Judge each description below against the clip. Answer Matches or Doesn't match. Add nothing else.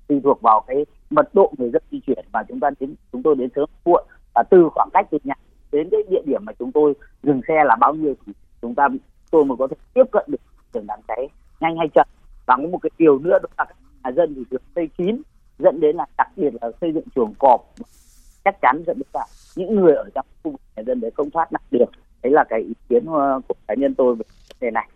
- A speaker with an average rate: Doesn't match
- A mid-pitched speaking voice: Matches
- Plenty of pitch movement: Matches